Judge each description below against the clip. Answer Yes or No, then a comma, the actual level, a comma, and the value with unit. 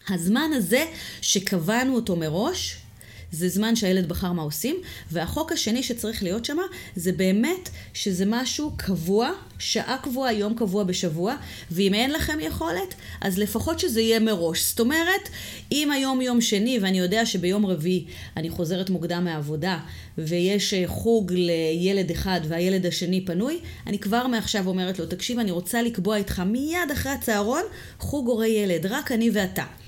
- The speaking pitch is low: No, high, 200 Hz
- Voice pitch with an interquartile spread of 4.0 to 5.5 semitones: Yes, average, 4.8 semitones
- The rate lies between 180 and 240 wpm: No, average, 150 wpm